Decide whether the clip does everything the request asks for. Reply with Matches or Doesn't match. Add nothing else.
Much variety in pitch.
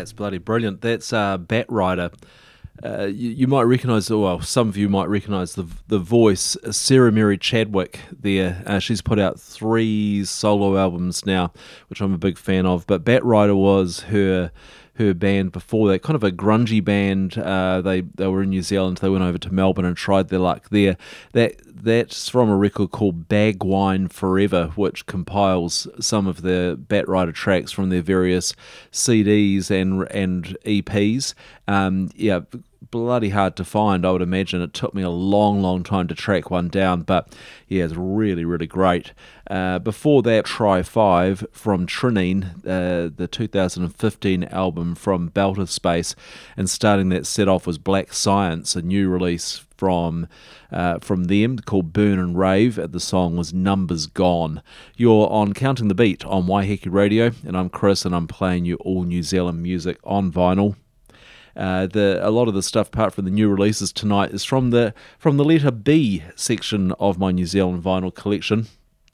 Doesn't match